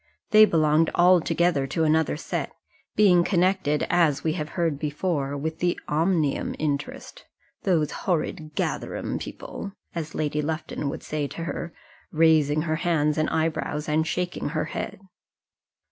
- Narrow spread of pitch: Yes, narrow, 2.3 semitones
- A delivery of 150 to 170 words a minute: No, average, 140 wpm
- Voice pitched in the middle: Yes, medium, 160 Hz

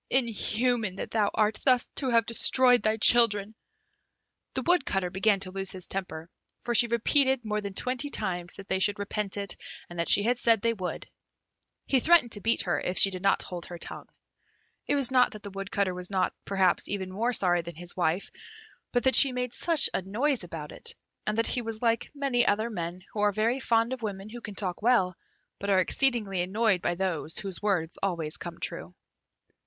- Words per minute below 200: No, fast, 205 wpm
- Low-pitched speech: No, high, 205 Hz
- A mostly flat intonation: No, average, 4.3 semitones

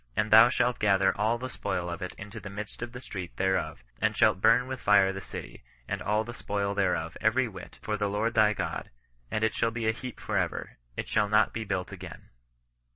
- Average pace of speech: No, fast, 230 wpm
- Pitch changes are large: No, average, 2.7 semitones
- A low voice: Yes, low, 105 Hz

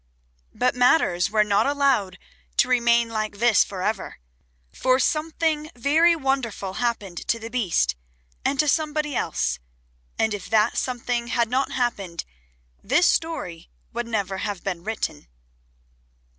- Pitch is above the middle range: Yes, high, 235 Hz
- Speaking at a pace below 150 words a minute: Yes, slow, 135 wpm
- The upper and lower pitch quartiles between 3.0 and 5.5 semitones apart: Yes, average, 5.0 semitones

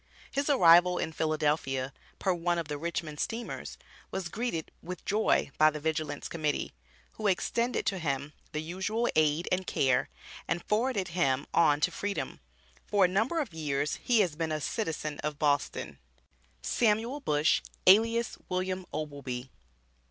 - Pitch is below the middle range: No, medium, 170 Hz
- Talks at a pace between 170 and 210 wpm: No, average, 150 wpm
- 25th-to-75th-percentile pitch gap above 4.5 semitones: Yes, average, 5.2 semitones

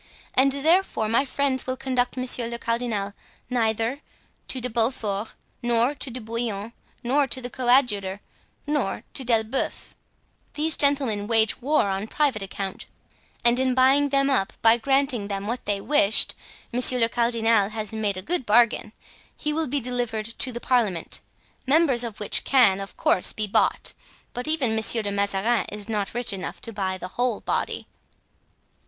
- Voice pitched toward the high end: Yes, high, 235 Hz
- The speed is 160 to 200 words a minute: Yes, average, 165 wpm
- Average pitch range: Yes, average, 3.6 semitones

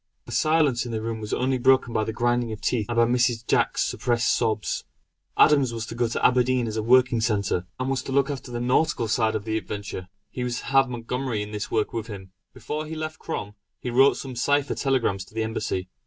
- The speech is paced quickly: Yes, fast, 230 wpm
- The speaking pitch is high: No, low, 120 Hz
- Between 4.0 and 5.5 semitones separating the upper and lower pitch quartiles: No, average, 2.9 semitones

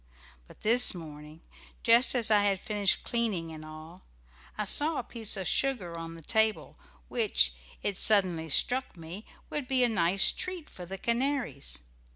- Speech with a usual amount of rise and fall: No, wide, 6.1 semitones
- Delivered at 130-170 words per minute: Yes, average, 165 wpm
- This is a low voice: No, high, 200 Hz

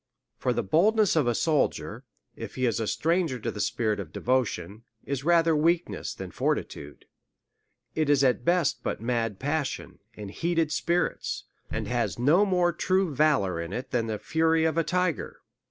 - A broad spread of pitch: Yes, wide, 6.0 semitones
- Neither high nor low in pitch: Yes, medium, 150 Hz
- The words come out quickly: No, average, 170 wpm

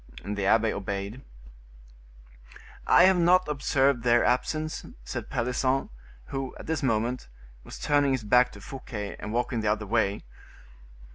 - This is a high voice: No, low, 125 Hz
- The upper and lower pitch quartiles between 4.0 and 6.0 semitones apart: Yes, average, 4.3 semitones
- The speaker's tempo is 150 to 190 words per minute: No, average, 140 wpm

